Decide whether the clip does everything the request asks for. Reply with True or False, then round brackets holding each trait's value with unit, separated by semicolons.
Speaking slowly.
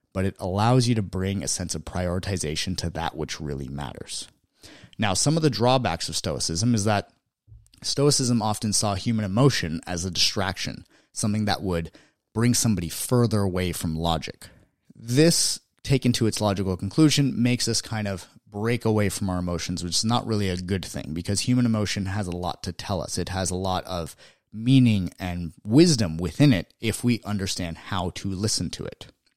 False (185 wpm)